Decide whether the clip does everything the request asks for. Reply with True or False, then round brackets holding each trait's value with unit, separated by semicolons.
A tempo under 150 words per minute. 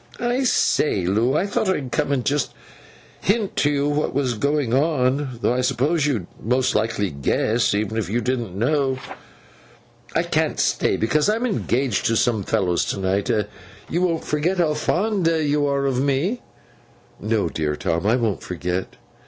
False (170 wpm)